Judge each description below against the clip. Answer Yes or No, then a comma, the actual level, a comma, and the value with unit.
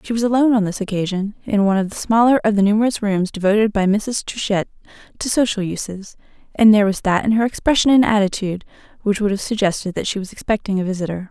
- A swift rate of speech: Yes, fast, 220 wpm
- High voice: Yes, high, 205 Hz